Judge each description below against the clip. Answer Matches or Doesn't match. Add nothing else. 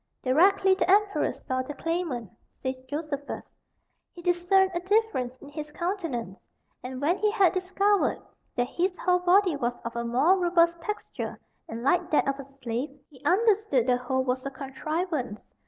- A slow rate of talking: Doesn't match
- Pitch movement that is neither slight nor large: Doesn't match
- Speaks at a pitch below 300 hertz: Doesn't match